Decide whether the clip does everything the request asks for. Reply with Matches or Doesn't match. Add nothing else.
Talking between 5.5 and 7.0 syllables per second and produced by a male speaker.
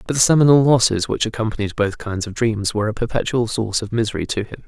Matches